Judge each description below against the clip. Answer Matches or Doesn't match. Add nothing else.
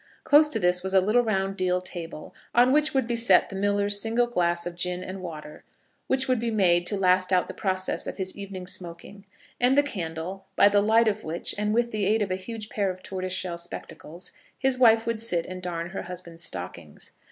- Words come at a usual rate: Doesn't match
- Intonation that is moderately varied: Matches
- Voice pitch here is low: Doesn't match